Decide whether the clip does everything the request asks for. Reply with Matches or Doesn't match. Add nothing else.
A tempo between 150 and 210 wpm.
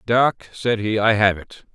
Matches